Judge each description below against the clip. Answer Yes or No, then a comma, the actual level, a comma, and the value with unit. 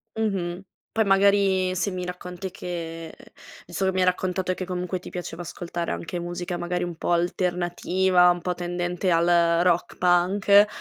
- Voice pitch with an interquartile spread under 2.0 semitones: Yes, narrow, 1.2 semitones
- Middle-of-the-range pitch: Yes, medium, 180 Hz